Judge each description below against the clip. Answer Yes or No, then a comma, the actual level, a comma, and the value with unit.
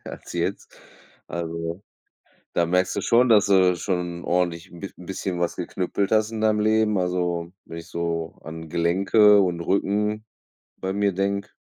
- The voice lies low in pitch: Yes, very low, 90 Hz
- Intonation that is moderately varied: Yes, average, 3.0 semitones